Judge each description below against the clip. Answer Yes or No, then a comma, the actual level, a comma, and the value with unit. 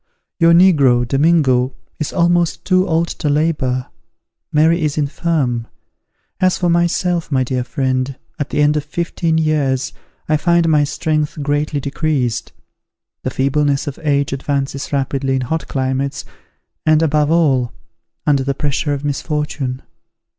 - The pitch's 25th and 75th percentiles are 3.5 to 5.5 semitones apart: No, average, 3.1 semitones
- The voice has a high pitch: No, medium, 145 Hz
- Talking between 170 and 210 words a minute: No, average, 140 wpm